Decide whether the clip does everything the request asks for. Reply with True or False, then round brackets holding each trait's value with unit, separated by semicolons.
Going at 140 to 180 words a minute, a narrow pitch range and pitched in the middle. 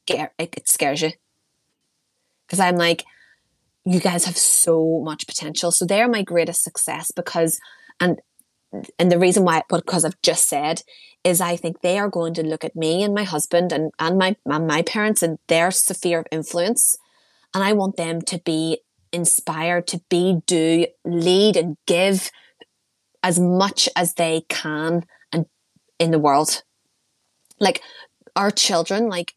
True (155 wpm; 2.3 semitones; 175 Hz)